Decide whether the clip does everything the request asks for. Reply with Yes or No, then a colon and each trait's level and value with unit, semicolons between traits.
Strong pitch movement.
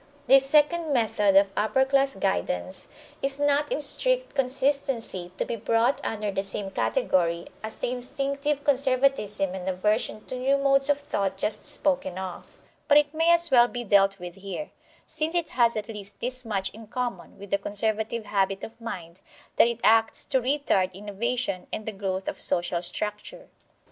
Yes: wide, 5.8 semitones